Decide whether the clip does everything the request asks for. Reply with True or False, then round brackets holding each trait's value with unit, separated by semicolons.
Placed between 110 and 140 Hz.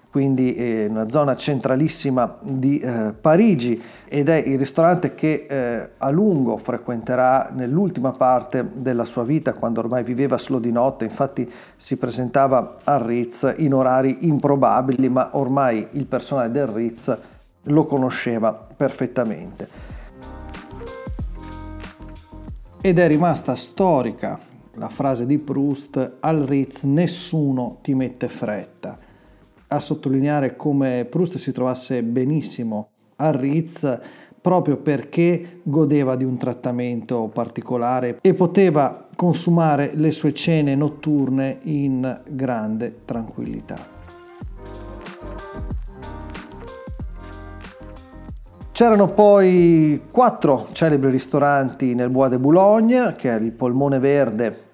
True (135 Hz)